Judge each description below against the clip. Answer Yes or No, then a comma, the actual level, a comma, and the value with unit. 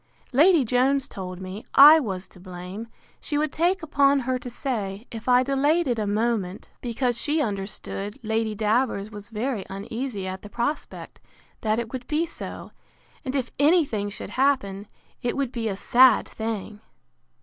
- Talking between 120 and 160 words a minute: No, average, 170 wpm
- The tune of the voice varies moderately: Yes, average, 5.0 semitones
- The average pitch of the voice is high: Yes, high, 235 Hz